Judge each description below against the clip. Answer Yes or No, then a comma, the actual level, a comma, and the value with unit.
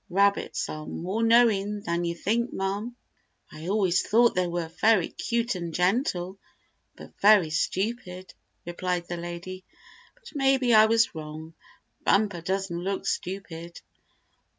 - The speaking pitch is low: No, high, 190 Hz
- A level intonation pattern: No, average, 4.0 semitones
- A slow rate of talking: Yes, slow, 130 wpm